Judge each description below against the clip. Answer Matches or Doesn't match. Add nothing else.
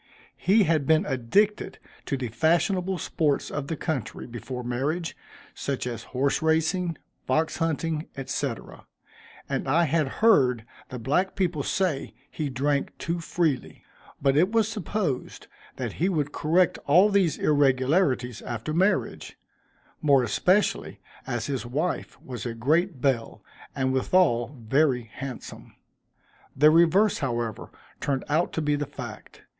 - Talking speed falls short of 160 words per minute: Matches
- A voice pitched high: Doesn't match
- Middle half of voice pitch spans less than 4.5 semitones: Doesn't match